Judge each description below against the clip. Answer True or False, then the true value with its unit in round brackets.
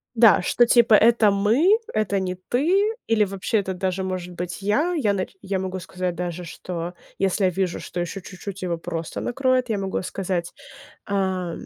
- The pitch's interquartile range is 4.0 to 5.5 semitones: False (3.5 semitones)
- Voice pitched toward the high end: True (195 Hz)